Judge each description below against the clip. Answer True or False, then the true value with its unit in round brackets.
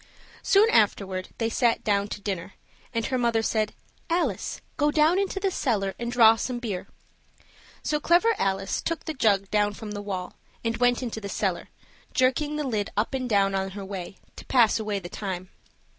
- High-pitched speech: True (220 Hz)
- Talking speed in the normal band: True (190 wpm)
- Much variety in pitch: False (4.4 semitones)